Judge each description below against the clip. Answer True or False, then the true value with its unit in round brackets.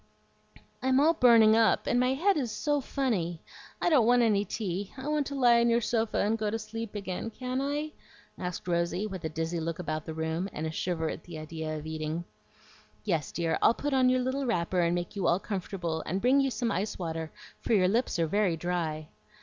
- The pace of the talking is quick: True (220 wpm)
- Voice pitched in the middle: False (205 Hz)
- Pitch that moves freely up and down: True (6.6 semitones)